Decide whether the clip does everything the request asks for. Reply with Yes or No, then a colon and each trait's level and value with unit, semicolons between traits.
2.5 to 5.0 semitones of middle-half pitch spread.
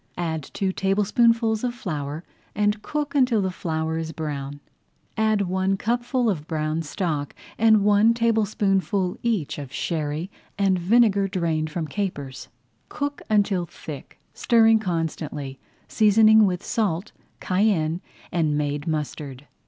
No: wide, 5.6 semitones